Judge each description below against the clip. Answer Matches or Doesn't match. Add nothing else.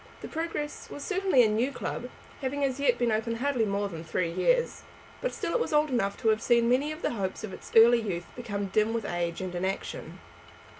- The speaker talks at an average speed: Doesn't match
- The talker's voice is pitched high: Matches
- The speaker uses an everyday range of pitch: Doesn't match